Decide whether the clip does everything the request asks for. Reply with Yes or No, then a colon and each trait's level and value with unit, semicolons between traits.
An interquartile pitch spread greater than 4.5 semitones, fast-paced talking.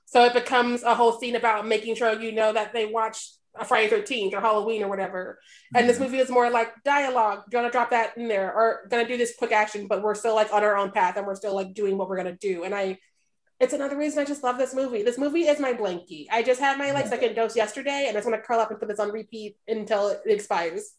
No: average, 3.3 semitones; fast, 270 wpm